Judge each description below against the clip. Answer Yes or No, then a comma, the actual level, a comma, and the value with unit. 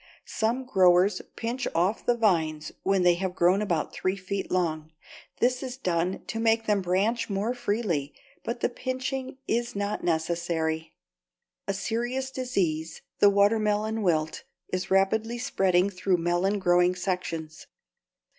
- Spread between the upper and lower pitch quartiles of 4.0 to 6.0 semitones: Yes, average, 4.3 semitones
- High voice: Yes, high, 195 Hz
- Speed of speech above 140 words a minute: No, slow, 135 wpm